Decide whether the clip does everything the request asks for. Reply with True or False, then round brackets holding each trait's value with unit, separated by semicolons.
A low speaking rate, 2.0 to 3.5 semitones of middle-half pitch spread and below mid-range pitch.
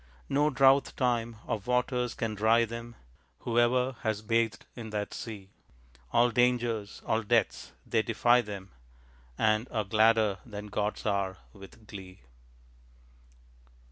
True (125 wpm; 2.4 semitones; 115 Hz)